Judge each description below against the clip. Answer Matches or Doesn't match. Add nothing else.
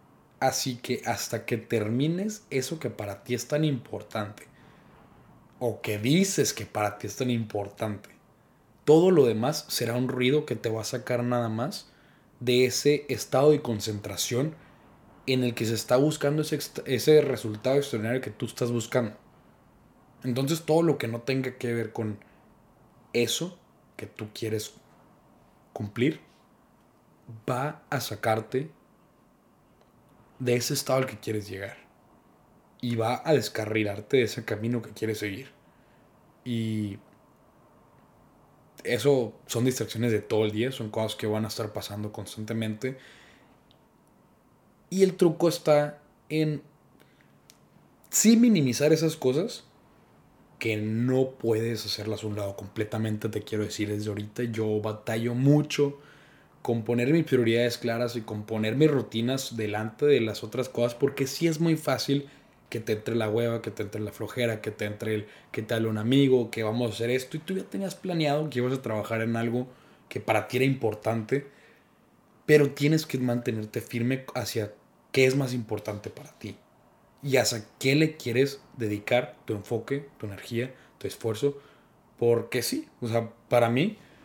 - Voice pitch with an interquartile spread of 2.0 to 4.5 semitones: Matches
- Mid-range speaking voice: Doesn't match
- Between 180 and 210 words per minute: Doesn't match